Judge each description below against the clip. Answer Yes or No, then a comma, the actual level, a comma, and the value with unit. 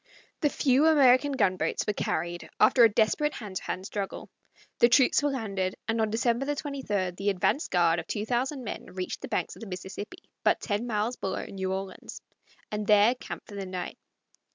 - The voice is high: Yes, high, 210 Hz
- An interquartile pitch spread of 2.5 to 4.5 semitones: No, average, 5.1 semitones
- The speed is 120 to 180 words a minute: No, average, 190 wpm